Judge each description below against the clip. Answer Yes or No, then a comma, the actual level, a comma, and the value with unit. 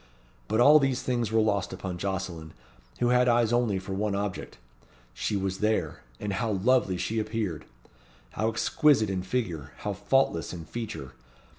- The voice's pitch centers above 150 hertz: No, low, 105 Hz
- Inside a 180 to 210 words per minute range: No, average, 160 wpm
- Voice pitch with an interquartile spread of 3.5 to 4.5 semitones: Yes, average, 4.0 semitones